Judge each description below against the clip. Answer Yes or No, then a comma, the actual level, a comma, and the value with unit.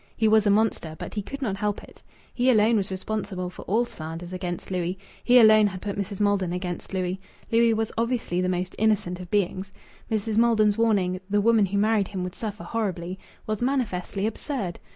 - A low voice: No, high, 205 Hz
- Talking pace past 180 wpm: Yes, average, 195 wpm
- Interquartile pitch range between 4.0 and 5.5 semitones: No, average, 3.2 semitones